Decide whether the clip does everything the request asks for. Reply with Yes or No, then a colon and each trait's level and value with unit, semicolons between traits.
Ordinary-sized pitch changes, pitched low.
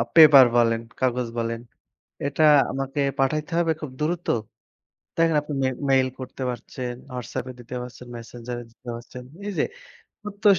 Yes: average, 3.8 semitones; low, 130 Hz